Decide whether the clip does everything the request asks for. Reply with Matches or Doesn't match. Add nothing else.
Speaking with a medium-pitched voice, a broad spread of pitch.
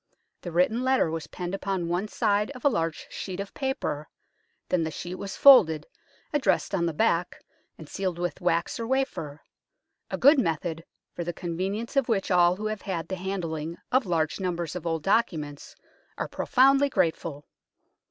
Doesn't match